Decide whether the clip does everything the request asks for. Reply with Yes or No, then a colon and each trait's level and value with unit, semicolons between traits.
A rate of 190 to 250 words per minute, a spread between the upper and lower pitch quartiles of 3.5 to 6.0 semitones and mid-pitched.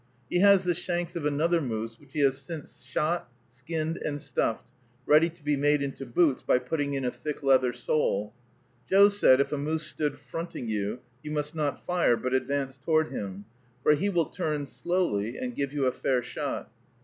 Yes: average, 195 wpm; average, 4.1 semitones; medium, 145 Hz